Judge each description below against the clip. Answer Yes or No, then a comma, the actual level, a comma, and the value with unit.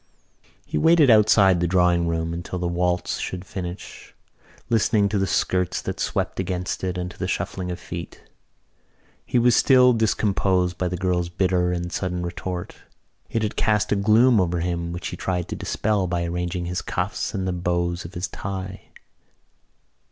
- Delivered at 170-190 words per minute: Yes, average, 175 wpm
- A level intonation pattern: Yes, narrow, 2.1 semitones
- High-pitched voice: No, very low, 90 Hz